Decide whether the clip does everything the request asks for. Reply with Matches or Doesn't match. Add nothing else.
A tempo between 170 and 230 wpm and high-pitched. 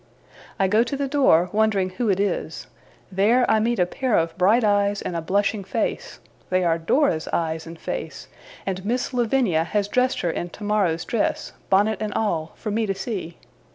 Matches